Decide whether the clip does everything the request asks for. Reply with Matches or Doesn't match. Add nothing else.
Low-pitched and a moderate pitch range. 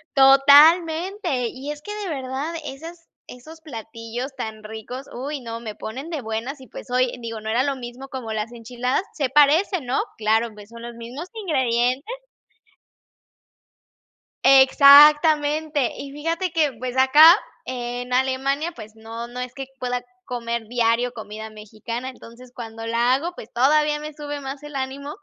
Doesn't match